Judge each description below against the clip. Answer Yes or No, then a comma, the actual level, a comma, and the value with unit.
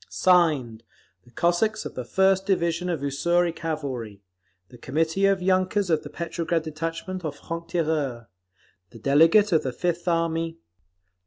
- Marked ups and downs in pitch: No, average, 3.5 semitones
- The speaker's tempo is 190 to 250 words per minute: No, average, 145 wpm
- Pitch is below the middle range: No, medium, 165 Hz